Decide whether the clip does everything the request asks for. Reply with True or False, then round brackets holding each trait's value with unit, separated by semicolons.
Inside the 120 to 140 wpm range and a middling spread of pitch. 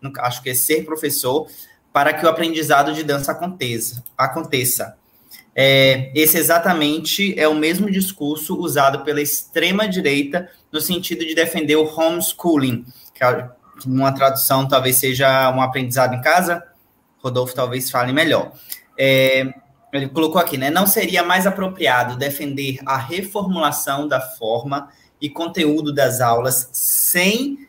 True (130 wpm; 4.0 semitones)